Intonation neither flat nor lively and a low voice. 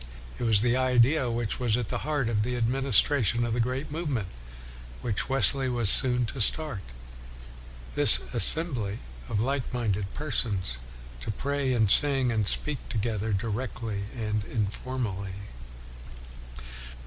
Yes: average, 3.7 semitones; low, 120 Hz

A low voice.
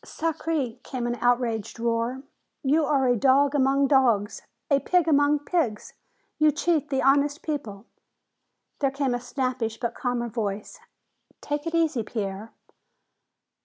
No: very high, 265 Hz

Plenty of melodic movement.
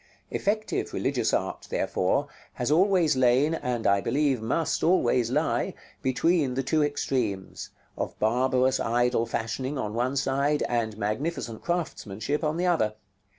No: average, 4.7 semitones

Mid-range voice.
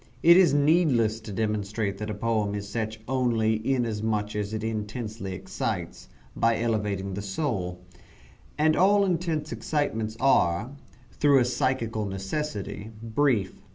No: low, 110 Hz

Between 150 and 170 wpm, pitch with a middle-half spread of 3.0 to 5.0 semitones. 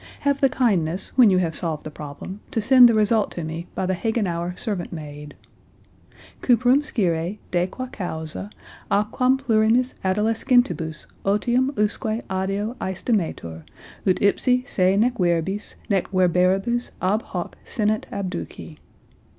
No: slow, 135 wpm; average, 4.7 semitones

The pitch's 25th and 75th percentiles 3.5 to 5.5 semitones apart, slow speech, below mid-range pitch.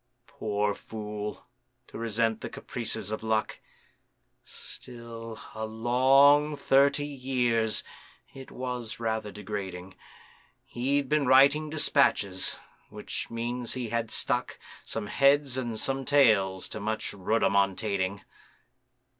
Yes: average, 4.0 semitones; slow, 105 wpm; low, 115 Hz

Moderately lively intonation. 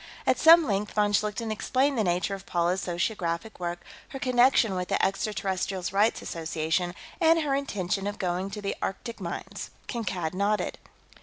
Yes: average, 4.0 semitones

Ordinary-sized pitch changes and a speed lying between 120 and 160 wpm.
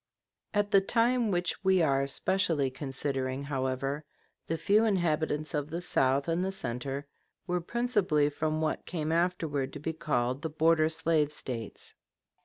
Yes: average, 4.4 semitones; average, 155 wpm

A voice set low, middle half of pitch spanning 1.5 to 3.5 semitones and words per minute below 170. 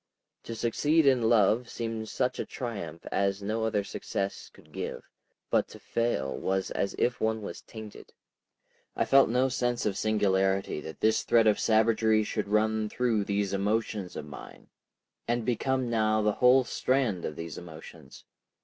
Yes: low, 110 Hz; average, 3.1 semitones; average, 160 wpm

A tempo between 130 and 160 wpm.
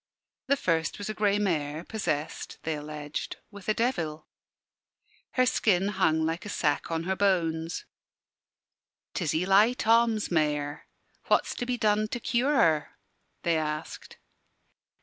Yes: slow, 135 wpm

